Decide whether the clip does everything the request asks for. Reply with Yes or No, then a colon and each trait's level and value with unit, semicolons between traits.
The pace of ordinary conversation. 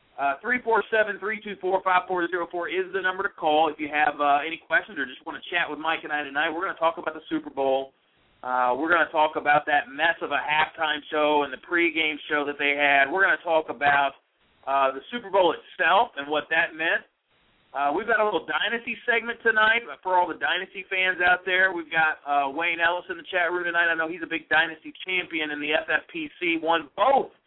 No: fast, 220 wpm